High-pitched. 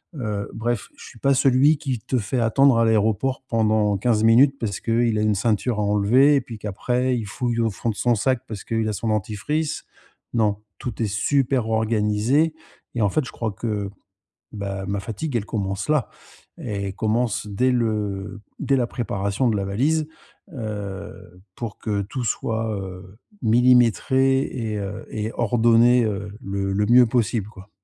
No: low, 110 Hz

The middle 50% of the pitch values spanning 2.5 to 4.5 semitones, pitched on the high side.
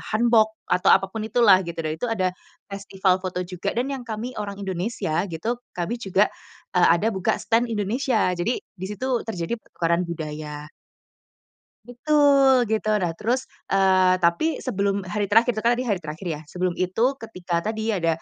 Yes: average, 4.2 semitones; high, 200 Hz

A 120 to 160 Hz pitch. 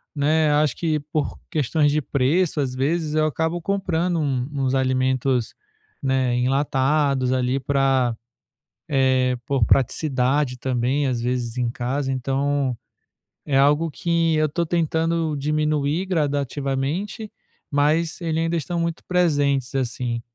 Yes: medium, 140 Hz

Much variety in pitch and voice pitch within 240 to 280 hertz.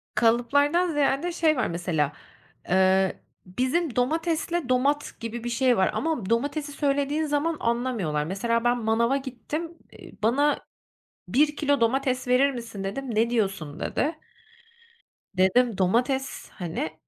No: average, 4.8 semitones; very high, 250 Hz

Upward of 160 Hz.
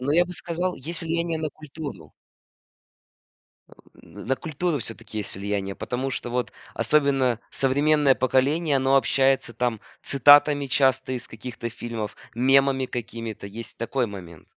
No: low, 135 Hz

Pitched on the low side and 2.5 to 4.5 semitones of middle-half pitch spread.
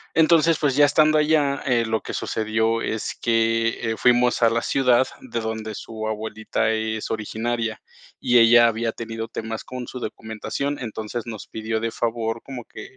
No: low, 115 Hz; narrow, 2.0 semitones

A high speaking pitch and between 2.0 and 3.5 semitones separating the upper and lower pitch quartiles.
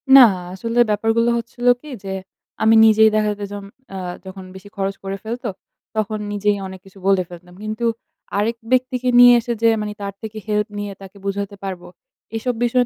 Yes: high, 210 Hz; average, 2.7 semitones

